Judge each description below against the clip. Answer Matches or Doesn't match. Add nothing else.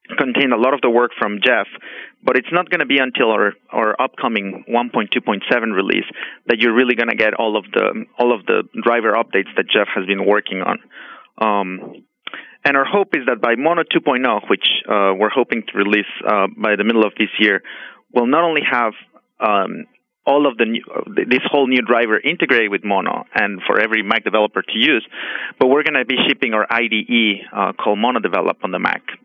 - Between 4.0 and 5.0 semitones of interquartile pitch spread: Doesn't match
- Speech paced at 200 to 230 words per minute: Matches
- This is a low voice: Matches